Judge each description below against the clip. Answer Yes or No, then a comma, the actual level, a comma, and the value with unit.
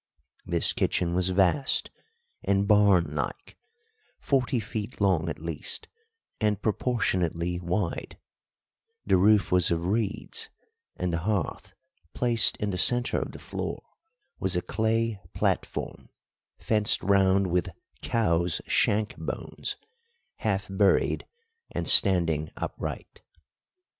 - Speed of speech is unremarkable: No, slow, 115 wpm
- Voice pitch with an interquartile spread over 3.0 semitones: Yes, average, 3.4 semitones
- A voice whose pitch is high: No, very low, 95 Hz